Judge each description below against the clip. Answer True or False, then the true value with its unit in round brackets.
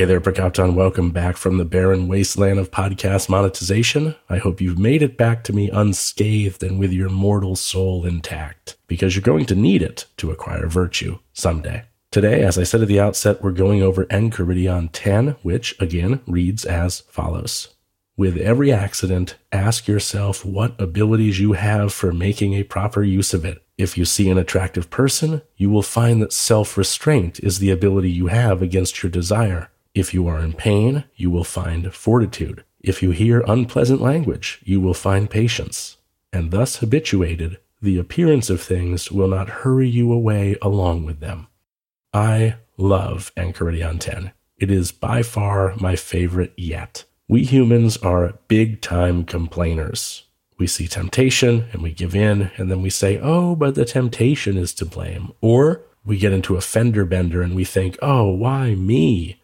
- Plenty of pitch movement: False (3.5 semitones)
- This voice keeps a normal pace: True (170 wpm)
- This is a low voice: True (95 Hz)